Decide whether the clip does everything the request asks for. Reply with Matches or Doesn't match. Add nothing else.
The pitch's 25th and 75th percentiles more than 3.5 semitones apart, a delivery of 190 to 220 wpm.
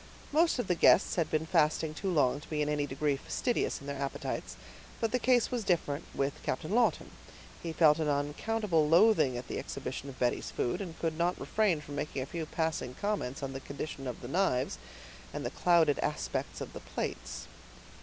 Matches